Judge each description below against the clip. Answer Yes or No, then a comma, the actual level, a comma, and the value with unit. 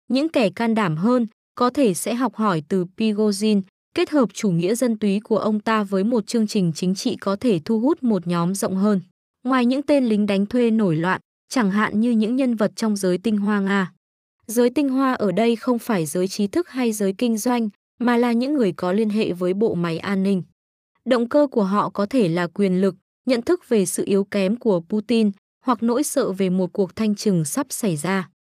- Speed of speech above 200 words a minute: Yes, average, 225 wpm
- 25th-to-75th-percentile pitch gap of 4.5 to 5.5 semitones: No, average, 4.0 semitones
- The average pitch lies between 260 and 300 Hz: No, high, 215 Hz